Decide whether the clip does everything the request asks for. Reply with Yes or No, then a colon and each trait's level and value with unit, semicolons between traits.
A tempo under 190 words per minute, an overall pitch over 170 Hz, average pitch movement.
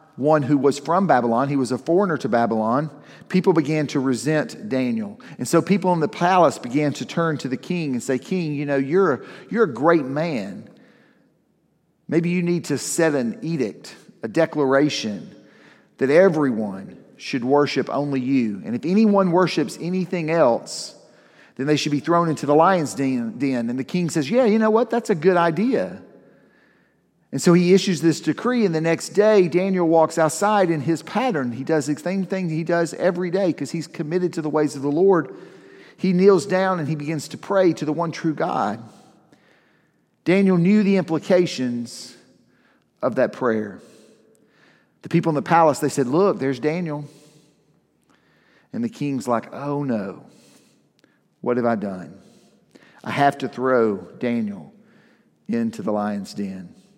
No: average, 170 wpm; medium, 160 Hz; average, 4.8 semitones